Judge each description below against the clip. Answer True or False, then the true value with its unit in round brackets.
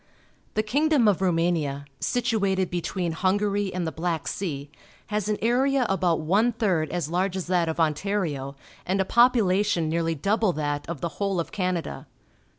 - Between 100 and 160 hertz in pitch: False (185 Hz)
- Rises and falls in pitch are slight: False (4.1 semitones)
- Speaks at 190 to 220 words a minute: False (170 wpm)